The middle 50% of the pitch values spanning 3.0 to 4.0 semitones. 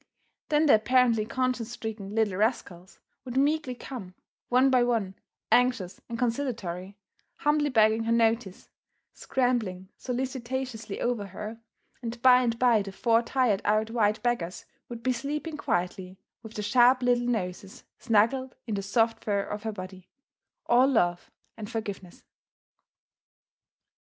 Yes: average, 3.6 semitones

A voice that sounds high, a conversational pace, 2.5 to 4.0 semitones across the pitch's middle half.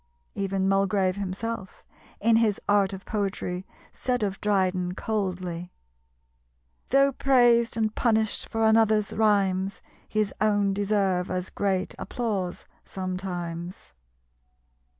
No: high, 200 Hz; slow, 105 wpm; average, 2.8 semitones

